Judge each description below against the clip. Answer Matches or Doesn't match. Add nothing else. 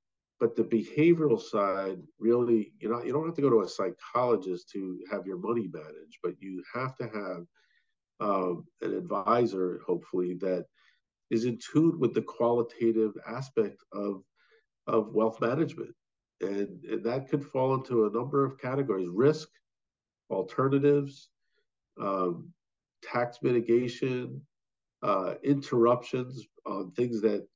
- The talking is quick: Doesn't match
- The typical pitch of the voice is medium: Doesn't match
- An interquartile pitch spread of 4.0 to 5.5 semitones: Matches